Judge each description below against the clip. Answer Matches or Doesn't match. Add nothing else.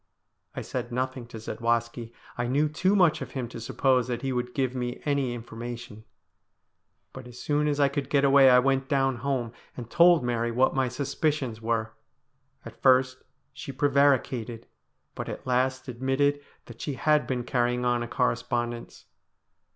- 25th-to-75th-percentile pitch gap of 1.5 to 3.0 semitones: Matches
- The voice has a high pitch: Doesn't match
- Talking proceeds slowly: Doesn't match